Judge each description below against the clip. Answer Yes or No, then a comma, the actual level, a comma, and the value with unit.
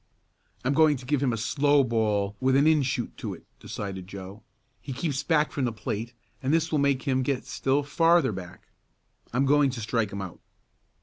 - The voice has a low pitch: Yes, low, 130 Hz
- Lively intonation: No, average, 4.6 semitones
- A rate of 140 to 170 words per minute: No, average, 200 wpm